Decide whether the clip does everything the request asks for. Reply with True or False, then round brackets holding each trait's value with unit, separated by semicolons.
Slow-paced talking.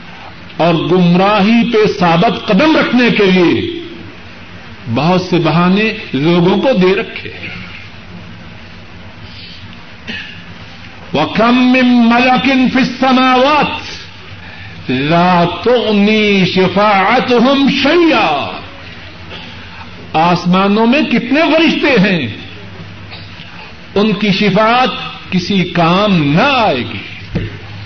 True (80 wpm)